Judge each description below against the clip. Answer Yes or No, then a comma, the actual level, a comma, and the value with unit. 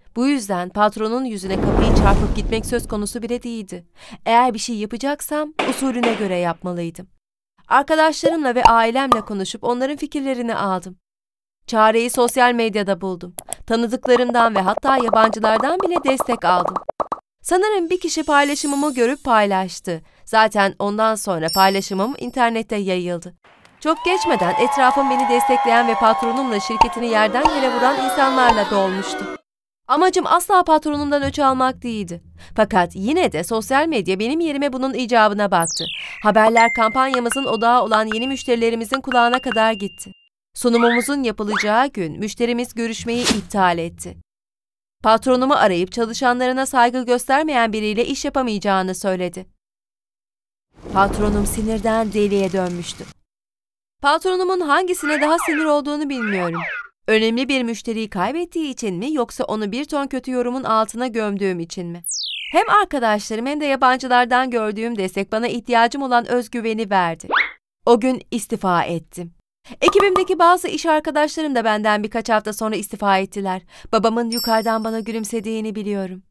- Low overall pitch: No, high, 230 Hz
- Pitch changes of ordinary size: Yes, average, 4.4 semitones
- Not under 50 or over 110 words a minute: No, average, 125 wpm